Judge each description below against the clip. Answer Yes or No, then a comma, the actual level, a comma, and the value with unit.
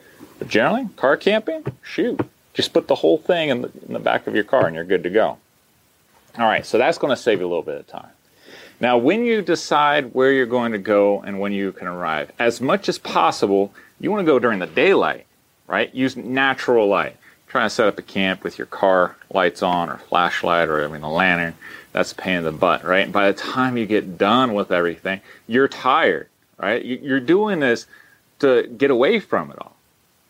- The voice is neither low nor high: No, low, 105 Hz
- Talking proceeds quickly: Yes, fast, 220 wpm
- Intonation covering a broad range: Yes, wide, 6.5 semitones